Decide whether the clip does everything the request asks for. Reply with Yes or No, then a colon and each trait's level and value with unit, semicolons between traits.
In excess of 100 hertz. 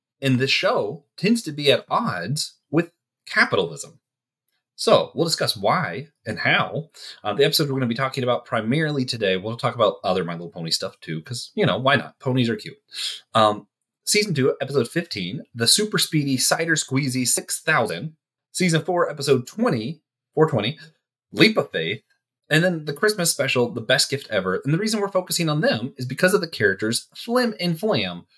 Yes: medium, 140 Hz